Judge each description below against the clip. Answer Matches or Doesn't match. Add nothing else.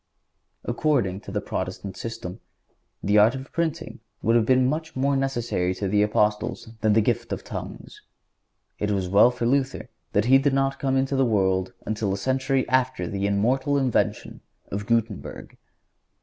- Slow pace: Doesn't match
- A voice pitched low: Matches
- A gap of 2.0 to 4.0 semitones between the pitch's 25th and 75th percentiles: Doesn't match